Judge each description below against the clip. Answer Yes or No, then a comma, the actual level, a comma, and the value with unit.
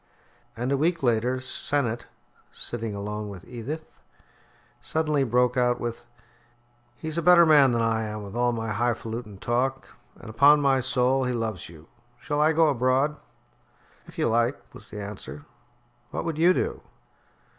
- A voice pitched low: Yes, low, 125 Hz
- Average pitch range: Yes, average, 4.1 semitones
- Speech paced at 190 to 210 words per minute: No, average, 160 wpm